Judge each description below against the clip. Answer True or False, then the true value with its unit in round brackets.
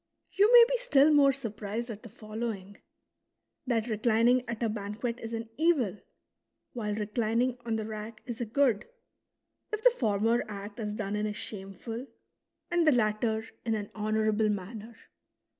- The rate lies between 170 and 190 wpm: False (160 wpm)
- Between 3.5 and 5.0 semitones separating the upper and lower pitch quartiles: False (2.6 semitones)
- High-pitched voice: True (225 Hz)